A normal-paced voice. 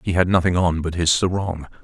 No: fast, 230 wpm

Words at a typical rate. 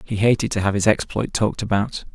No: fast, 225 wpm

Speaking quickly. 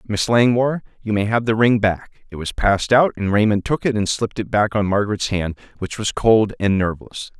Yes: fast, 225 wpm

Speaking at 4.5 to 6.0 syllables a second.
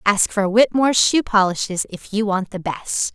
Yes: 5.0 syllables/s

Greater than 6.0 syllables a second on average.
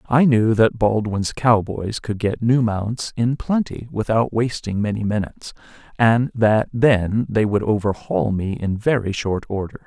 No: 4.2 syllables/s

